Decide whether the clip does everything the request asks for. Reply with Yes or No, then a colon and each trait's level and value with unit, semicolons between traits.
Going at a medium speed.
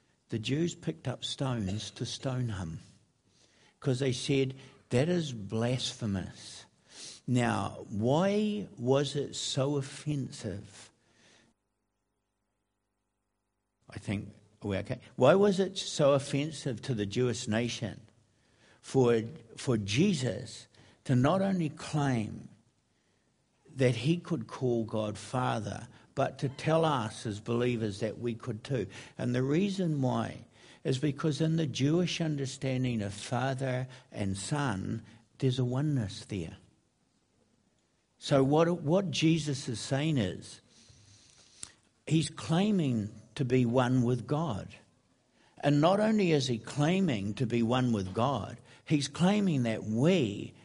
No: slow, 120 wpm